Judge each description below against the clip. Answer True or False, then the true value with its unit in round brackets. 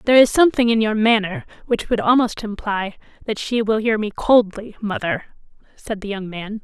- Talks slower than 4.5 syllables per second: False (5.2 syllables/s)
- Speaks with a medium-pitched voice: False (220 Hz)